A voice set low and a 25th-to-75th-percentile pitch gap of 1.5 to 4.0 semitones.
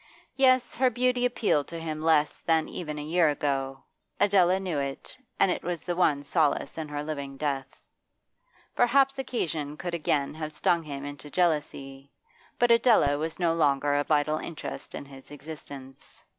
No: medium, 155 Hz; average, 3.7 semitones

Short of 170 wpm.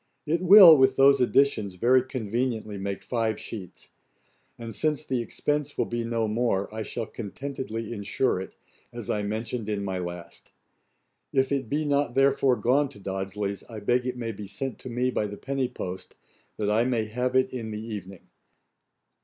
No: average, 175 wpm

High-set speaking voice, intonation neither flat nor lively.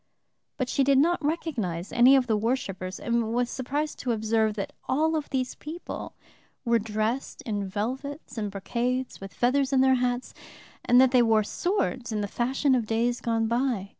Yes: high, 245 Hz; average, 3.4 semitones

